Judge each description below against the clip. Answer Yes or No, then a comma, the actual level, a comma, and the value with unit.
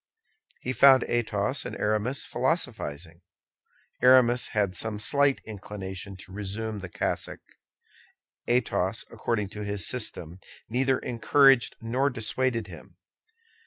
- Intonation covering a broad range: No, average, 4.2 semitones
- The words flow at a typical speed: No, slow, 110 wpm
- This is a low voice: Yes, low, 110 Hz